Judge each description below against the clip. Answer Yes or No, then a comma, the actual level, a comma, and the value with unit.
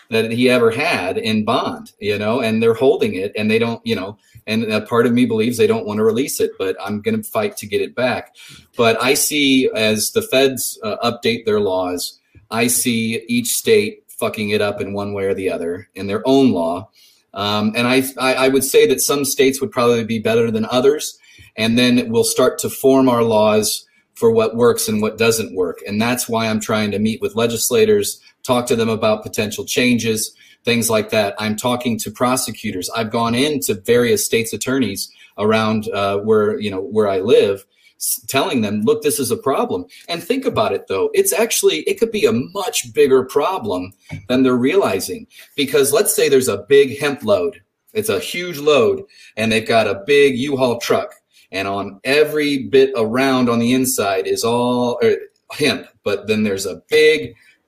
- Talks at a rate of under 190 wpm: No, average, 200 wpm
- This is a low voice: No, medium, 175 Hz